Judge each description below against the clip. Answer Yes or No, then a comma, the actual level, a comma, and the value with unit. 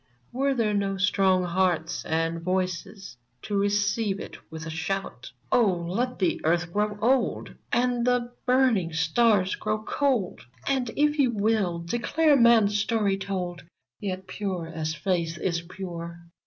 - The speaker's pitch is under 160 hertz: No, high, 195 Hz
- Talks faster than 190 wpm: No, average, 145 wpm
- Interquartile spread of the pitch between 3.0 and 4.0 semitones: No, average, 4.9 semitones